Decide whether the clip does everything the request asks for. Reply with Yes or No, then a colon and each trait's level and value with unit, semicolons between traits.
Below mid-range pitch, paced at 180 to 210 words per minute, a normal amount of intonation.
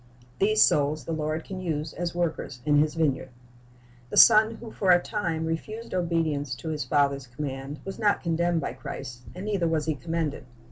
No: medium, 160 Hz; average, 190 wpm; average, 3.3 semitones